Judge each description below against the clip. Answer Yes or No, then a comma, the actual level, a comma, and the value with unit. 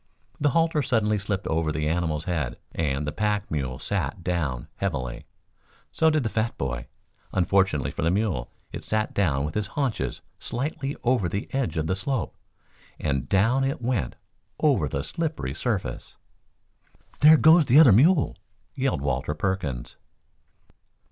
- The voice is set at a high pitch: No, very low, 95 Hz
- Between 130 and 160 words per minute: Yes, average, 150 wpm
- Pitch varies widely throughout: Yes, wide, 9.0 semitones